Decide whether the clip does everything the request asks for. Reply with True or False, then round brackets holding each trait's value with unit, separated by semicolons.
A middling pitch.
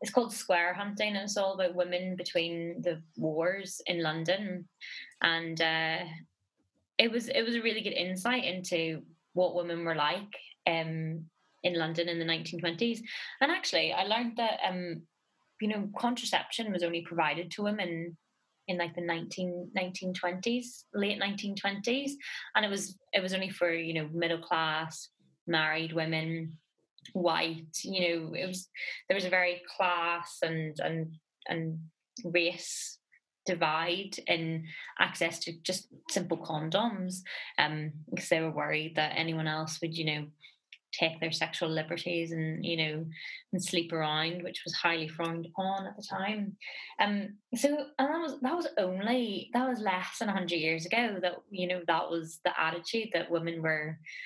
True (175 Hz)